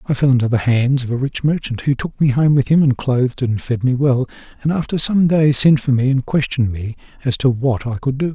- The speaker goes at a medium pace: No, fast, 265 wpm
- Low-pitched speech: Yes, low, 130 Hz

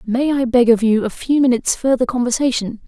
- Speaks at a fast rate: Yes, fast, 210 wpm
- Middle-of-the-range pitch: No, high, 245 Hz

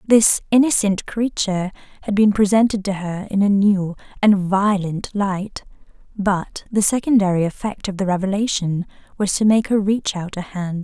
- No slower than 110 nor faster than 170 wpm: Yes, average, 160 wpm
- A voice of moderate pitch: No, high, 200 Hz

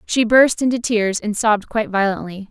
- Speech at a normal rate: Yes, average, 190 wpm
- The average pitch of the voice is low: No, high, 215 Hz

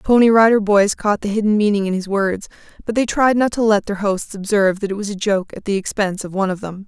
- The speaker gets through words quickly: Yes, fast, 280 wpm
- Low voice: No, high, 205 Hz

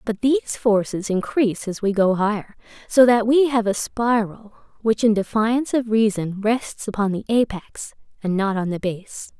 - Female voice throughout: Yes, female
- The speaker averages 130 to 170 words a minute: No, average, 180 wpm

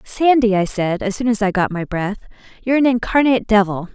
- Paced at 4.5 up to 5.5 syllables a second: No, 5.8 syllables/s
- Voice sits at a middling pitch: No, high, 215 Hz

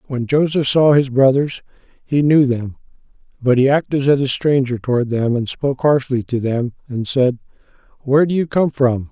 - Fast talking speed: No, average, 185 wpm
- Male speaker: Yes, male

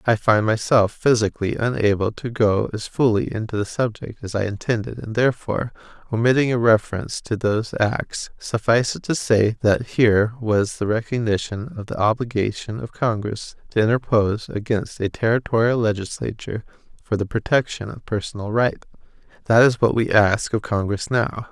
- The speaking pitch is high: No, low, 110 Hz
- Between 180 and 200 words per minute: No, average, 160 wpm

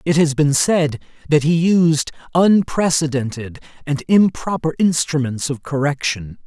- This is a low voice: No, medium, 150 Hz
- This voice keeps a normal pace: No, slow, 120 wpm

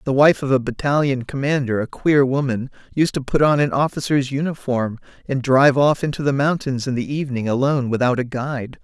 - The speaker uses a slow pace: No, average, 195 wpm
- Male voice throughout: Yes, male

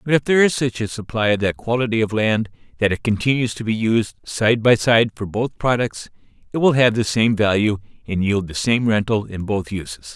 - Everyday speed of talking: No, fast, 225 wpm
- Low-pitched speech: Yes, low, 110 Hz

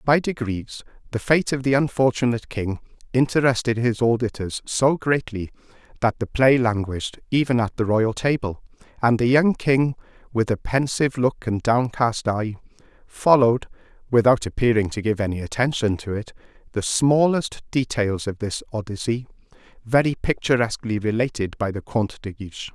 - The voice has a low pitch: Yes, low, 120 Hz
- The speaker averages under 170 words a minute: Yes, average, 150 wpm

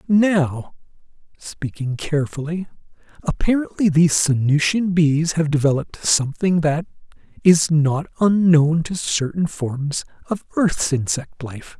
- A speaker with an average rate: No, slow, 105 wpm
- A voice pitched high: No, medium, 160 Hz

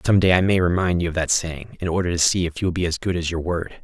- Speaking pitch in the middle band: No, very low, 85 Hz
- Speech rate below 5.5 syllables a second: No, 6.6 syllables/s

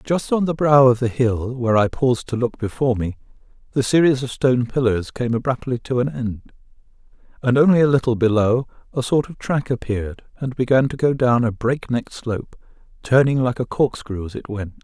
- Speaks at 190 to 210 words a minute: Yes, average, 200 wpm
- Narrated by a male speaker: Yes, male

